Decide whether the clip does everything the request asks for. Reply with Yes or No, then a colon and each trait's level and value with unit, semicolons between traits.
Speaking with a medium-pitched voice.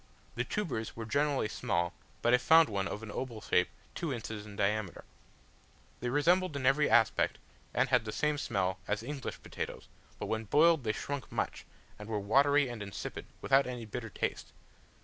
No: low, 120 Hz